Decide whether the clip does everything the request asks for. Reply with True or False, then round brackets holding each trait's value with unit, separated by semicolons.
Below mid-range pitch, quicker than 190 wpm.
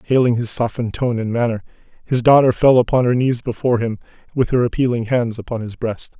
True (120 Hz; 205 wpm)